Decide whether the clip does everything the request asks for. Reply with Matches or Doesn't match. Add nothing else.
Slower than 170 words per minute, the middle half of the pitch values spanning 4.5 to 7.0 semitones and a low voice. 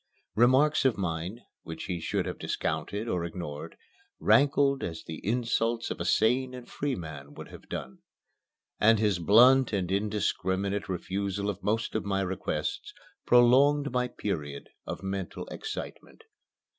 Matches